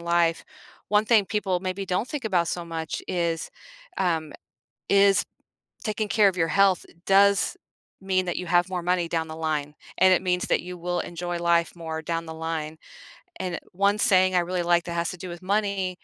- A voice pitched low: No, medium, 180 Hz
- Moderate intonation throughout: No, narrow, 2.3 semitones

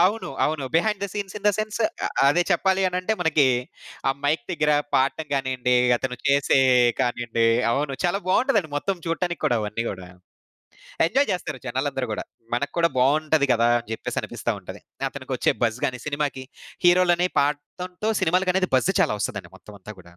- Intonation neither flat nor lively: No, wide, 5.8 semitones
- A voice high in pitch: No, medium, 150 Hz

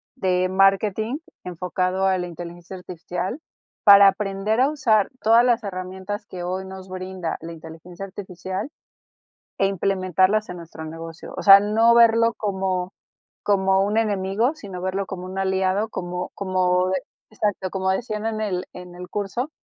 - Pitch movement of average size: No, narrow, 2.2 semitones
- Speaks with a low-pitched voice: No, high, 190 Hz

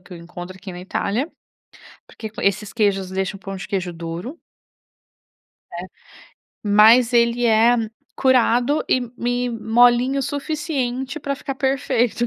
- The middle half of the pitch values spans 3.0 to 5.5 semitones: Yes, average, 4.7 semitones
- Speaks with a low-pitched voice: No, high, 235 Hz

